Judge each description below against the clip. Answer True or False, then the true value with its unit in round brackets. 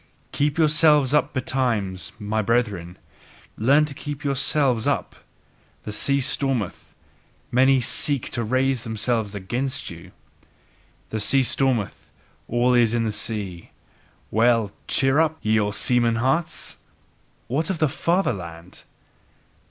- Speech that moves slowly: True (120 wpm)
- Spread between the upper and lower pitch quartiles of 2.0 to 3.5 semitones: False (4.3 semitones)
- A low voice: True (120 Hz)